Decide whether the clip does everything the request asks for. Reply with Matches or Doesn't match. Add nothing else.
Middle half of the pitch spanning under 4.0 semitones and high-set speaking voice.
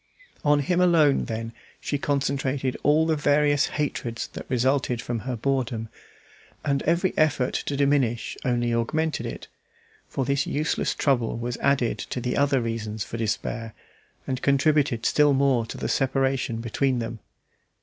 Doesn't match